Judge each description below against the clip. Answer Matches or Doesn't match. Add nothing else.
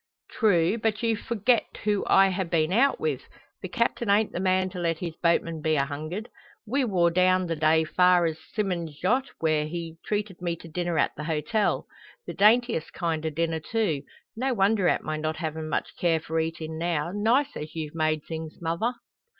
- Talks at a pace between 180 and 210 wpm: Matches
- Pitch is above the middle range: Doesn't match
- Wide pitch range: Doesn't match